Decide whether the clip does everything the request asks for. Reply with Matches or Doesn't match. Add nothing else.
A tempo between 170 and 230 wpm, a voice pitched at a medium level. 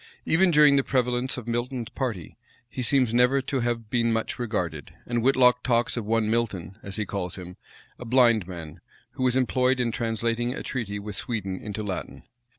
Doesn't match